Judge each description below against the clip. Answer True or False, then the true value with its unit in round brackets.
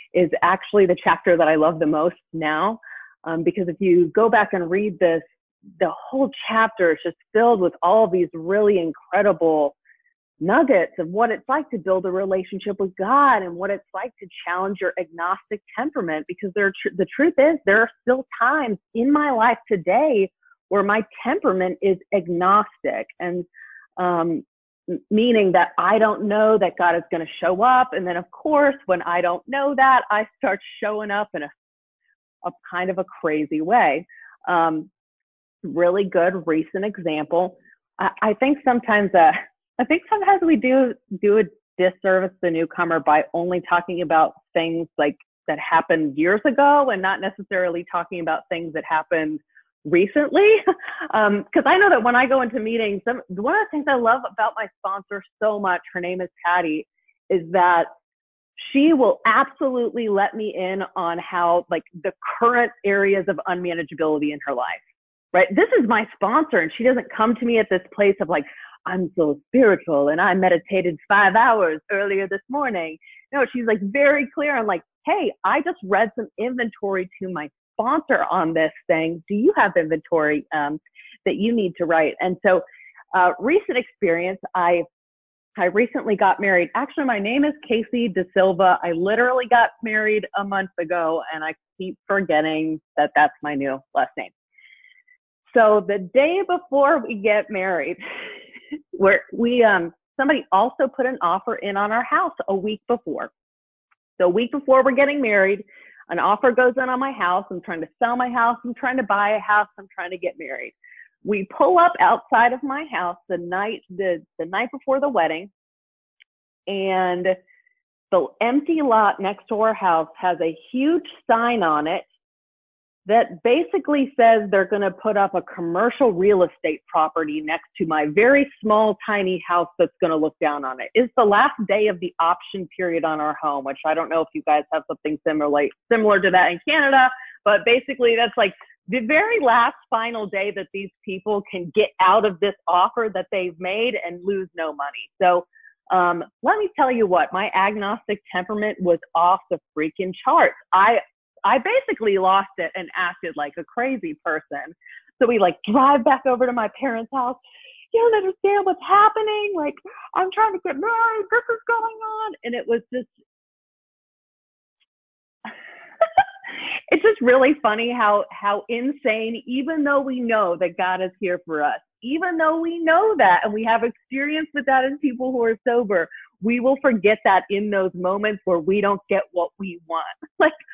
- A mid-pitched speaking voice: False (205 Hz)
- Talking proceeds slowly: False (180 wpm)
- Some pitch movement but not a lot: False (6.3 semitones)